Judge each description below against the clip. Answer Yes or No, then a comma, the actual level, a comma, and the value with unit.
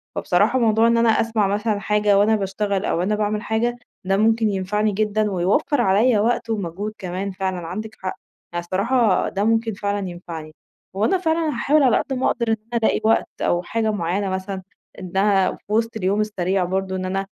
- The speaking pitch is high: Yes, high, 210 Hz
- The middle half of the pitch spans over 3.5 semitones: No, average, 2.9 semitones